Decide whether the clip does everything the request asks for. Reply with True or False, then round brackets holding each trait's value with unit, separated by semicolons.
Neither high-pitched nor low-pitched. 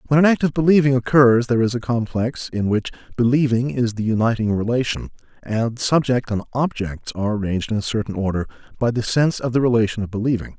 False (120 Hz)